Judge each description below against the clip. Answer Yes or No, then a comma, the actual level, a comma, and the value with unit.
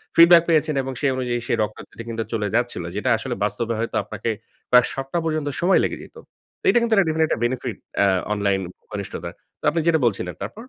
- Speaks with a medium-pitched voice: No, low, 125 Hz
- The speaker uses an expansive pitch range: Yes, wide, 6.0 semitones